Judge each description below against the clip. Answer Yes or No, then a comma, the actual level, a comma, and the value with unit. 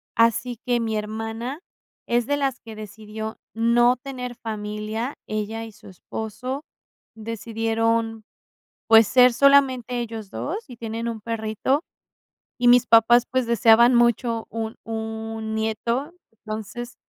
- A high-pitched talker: Yes, high, 230 Hz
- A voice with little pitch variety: Yes, narrow, 1.7 semitones